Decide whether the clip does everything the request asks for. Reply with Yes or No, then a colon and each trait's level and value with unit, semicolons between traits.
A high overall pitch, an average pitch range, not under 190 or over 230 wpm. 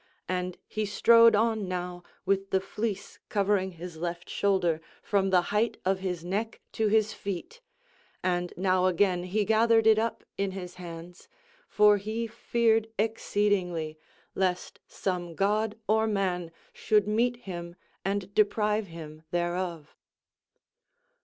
No: high, 195 Hz; average, 3.3 semitones; slow, 135 wpm